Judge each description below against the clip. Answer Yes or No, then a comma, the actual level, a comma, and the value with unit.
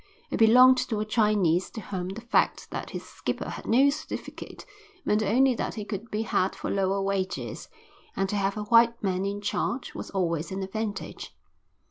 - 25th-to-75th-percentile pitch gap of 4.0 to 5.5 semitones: No, average, 3.0 semitones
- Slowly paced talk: No, average, 185 wpm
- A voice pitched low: No, high, 210 Hz